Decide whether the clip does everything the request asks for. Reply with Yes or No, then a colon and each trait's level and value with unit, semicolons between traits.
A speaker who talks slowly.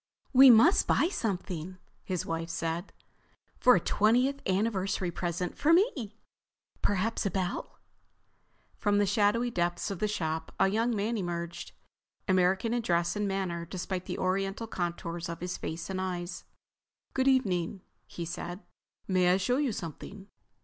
No: average, 150 wpm